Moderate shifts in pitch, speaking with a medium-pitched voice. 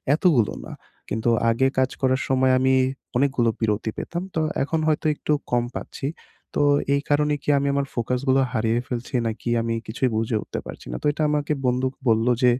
No: average, 3.4 semitones; low, 130 Hz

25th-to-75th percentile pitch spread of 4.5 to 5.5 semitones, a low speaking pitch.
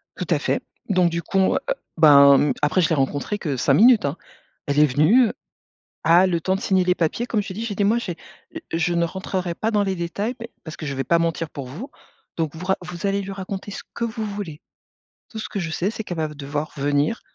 No: average, 4.8 semitones; medium, 175 Hz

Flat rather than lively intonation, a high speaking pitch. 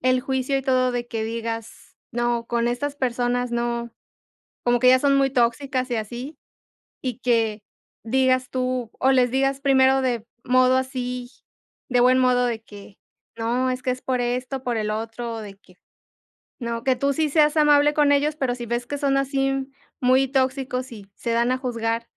Yes: narrow, 2.0 semitones; very high, 250 Hz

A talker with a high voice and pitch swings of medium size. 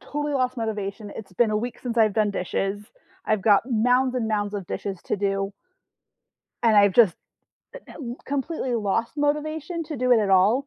Yes: high, 225 Hz; average, 4.0 semitones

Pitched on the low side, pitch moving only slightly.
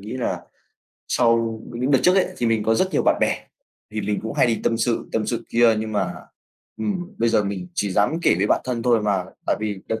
Yes: low, 115 Hz; narrow, 2.1 semitones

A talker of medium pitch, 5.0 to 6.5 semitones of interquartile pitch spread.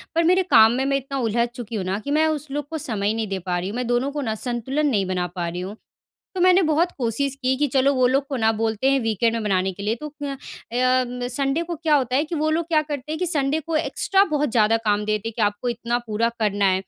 No: very high, 250 Hz; average, 5.3 semitones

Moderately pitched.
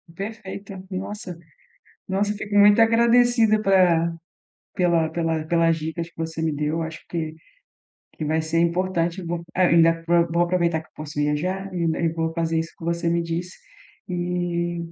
Yes: medium, 170 Hz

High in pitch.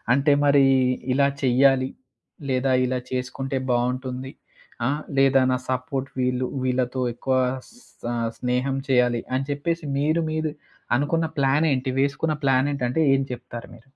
No: low, 135 Hz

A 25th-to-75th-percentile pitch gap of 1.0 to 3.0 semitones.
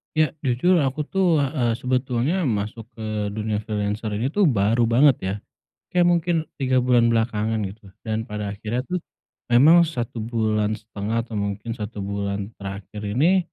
No: average, 4.2 semitones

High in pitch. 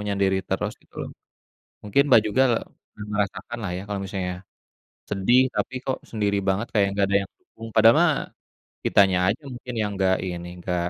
No: low, 100 Hz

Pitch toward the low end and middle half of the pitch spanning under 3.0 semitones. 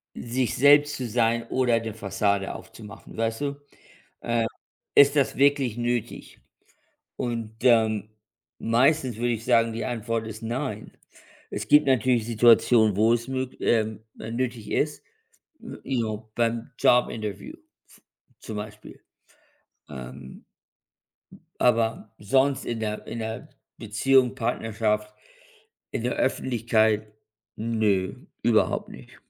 Yes: low, 115 Hz; narrow, 2.4 semitones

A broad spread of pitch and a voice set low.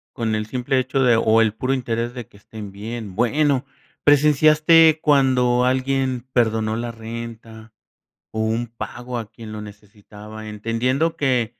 No: average, 2.9 semitones; low, 115 Hz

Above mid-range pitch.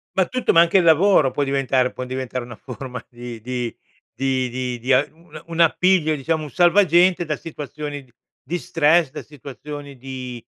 No: medium, 145 Hz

